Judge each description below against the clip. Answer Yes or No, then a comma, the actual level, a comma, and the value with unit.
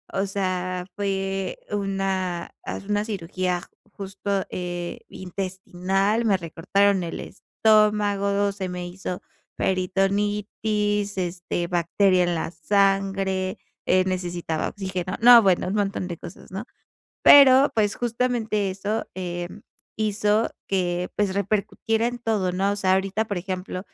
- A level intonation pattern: Yes, narrow, 2.1 semitones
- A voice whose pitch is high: Yes, high, 195 Hz